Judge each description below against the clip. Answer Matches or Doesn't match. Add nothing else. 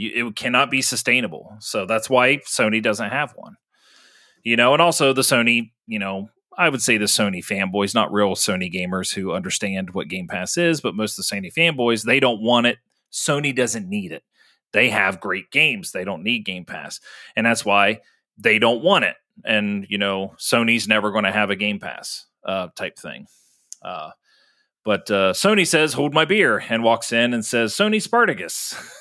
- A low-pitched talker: Matches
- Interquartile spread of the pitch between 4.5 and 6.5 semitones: Matches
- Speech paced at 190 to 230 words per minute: Matches